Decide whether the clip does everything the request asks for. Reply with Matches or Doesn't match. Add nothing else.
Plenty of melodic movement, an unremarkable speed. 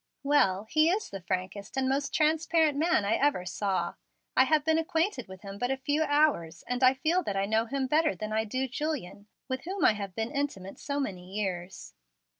Doesn't match